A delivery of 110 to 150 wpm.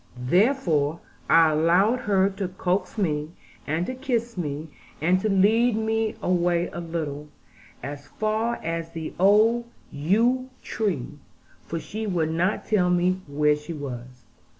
Yes: average, 140 wpm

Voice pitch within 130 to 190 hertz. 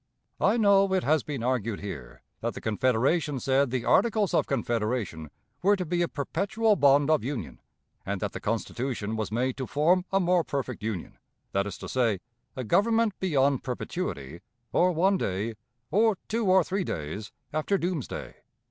Yes: medium, 140 Hz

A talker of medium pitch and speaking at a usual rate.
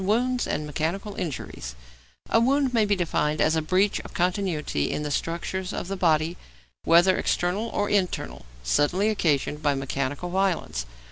Yes: medium, 175 Hz; average, 160 wpm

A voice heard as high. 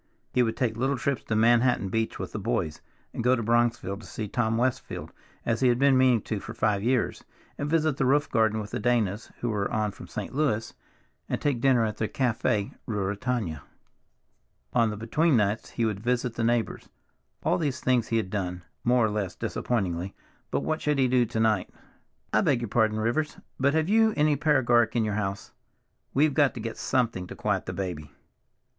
No: low, 115 Hz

